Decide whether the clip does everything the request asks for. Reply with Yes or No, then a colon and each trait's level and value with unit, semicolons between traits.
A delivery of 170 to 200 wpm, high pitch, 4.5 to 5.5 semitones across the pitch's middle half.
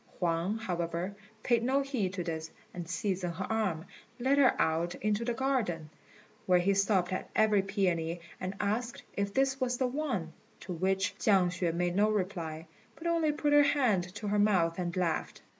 Yes: average, 180 wpm; high, 195 Hz; average, 5.0 semitones